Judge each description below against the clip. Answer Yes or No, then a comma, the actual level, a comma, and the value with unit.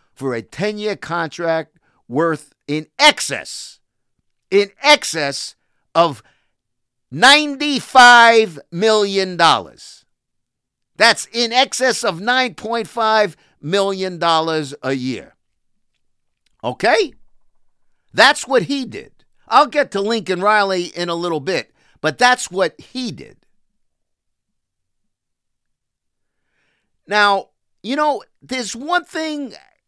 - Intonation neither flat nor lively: No, wide, 7.1 semitones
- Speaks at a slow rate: Yes, slow, 90 wpm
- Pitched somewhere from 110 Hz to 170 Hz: No, high, 205 Hz